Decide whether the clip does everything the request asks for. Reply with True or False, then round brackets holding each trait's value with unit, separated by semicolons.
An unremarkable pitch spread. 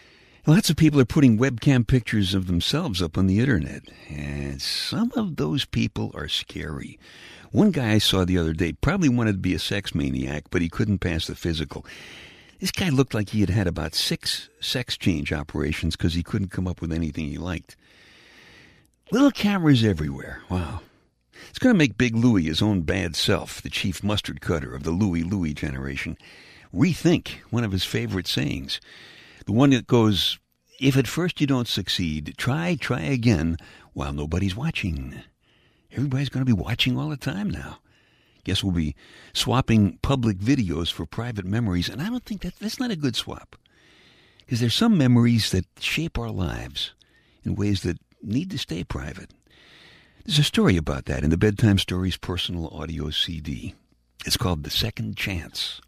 False (7.2 semitones)